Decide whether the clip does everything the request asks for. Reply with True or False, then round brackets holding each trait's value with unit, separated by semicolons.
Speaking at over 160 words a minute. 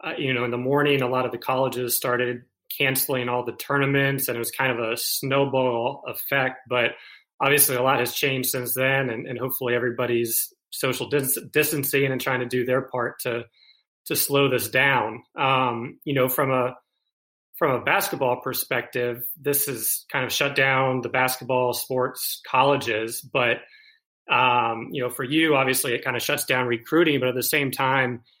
True (185 wpm)